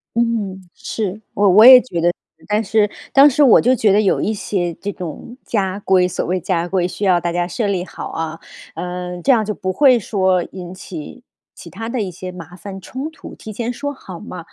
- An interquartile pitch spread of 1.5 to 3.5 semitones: No, average, 4.0 semitones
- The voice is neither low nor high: No, high, 195 Hz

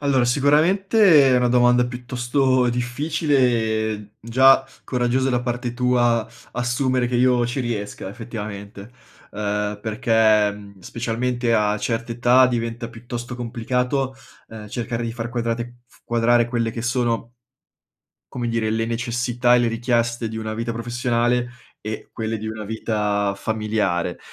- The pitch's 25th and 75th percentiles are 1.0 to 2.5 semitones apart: Yes, narrow, 1.8 semitones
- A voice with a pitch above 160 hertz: No, low, 120 Hz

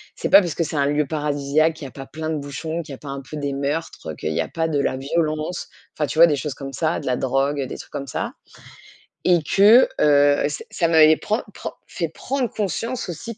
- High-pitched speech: No, medium, 150 Hz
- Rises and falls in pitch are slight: No, average, 3.0 semitones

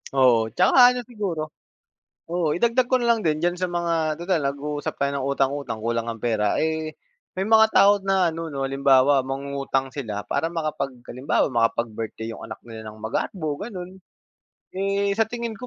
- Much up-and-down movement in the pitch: Yes, wide, 6.1 semitones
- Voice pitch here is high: No, medium, 155 Hz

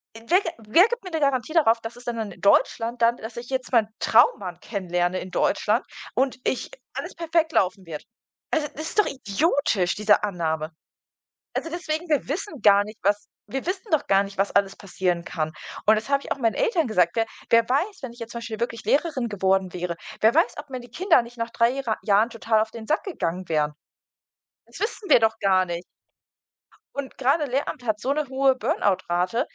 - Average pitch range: No, wide, 5.8 semitones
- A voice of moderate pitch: No, high, 230 Hz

